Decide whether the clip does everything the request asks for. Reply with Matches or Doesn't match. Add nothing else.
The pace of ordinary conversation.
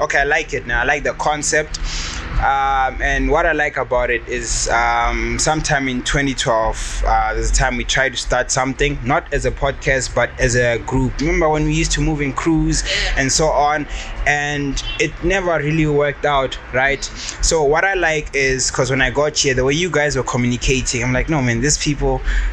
Doesn't match